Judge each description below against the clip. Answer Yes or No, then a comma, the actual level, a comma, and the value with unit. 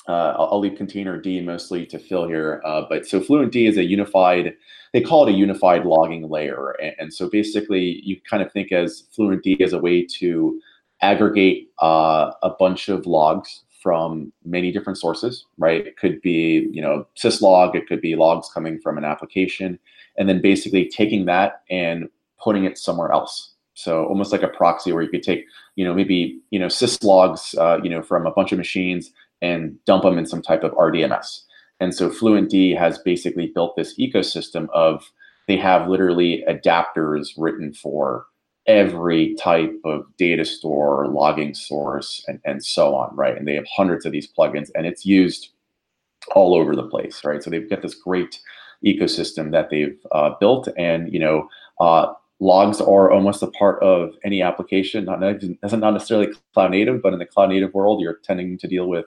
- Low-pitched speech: Yes, very low, 90 Hz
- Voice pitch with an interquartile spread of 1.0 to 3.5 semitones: Yes, average, 3.0 semitones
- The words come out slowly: No, average, 185 wpm